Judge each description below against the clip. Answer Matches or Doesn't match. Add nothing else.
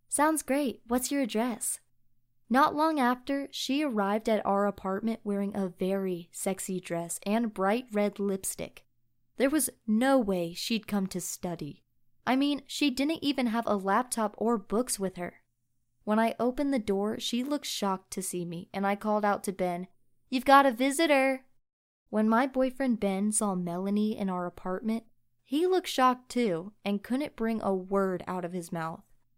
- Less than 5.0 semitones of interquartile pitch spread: Doesn't match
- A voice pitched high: Matches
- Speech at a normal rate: Matches